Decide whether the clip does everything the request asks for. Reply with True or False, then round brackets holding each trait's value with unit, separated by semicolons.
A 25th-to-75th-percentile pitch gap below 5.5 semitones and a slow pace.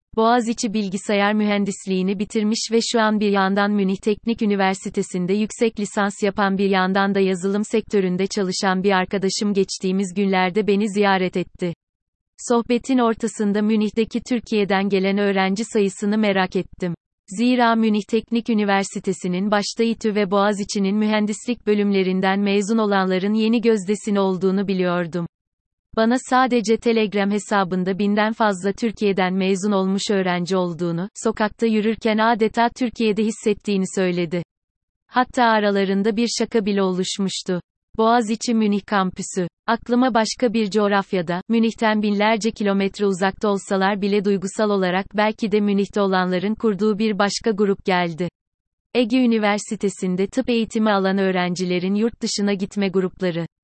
False (2.4 semitones; 125 wpm)